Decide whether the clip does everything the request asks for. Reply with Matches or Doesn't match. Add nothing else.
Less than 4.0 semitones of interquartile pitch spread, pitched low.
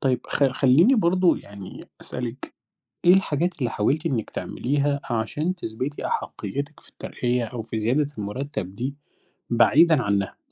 Doesn't match